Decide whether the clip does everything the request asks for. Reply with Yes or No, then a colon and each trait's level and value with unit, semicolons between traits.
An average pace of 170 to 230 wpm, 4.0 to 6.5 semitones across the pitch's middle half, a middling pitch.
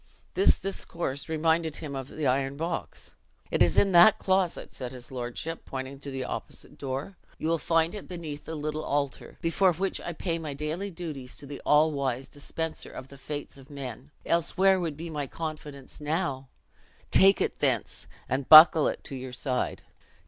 No: average, 180 wpm; average, 3.5 semitones; medium, 150 Hz